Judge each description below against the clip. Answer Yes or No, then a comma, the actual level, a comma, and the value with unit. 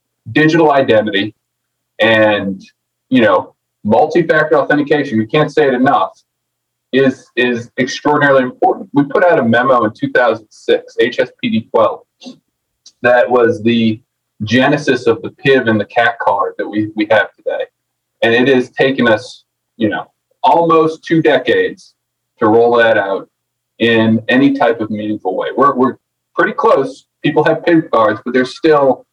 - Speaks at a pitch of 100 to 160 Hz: Yes, low, 135 Hz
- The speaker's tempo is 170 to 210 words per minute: No, average, 145 wpm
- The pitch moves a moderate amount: No, wide, 6.3 semitones